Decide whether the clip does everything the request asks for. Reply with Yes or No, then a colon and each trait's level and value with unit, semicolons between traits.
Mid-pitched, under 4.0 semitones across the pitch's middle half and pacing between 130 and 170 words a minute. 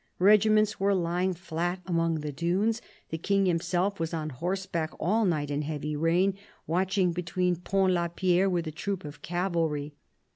Yes: medium, 175 Hz; average, 2.8 semitones; average, 160 wpm